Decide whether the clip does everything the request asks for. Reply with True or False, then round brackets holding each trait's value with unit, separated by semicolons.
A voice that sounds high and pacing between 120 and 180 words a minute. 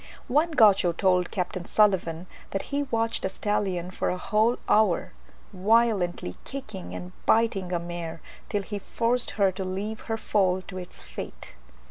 True (195 Hz; 160 wpm)